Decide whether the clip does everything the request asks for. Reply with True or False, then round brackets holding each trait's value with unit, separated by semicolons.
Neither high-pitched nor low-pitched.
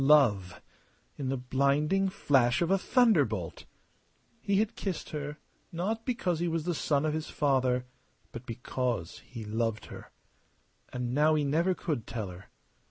True (145 Hz)